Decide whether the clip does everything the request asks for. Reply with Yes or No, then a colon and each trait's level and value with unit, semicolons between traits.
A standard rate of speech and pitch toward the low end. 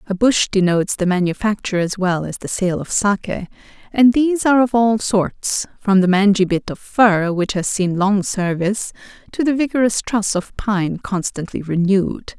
No: average, 180 wpm; high, 200 Hz